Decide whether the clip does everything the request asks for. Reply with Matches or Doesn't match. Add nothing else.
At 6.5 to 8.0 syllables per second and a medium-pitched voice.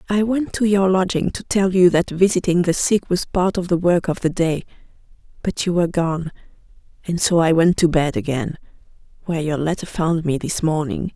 Doesn't match